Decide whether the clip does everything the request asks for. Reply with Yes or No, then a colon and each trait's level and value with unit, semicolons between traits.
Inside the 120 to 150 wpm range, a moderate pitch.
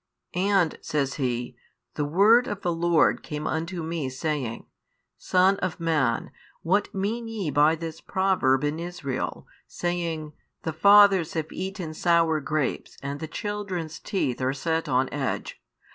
Yes: average, 145 wpm; medium, 165 Hz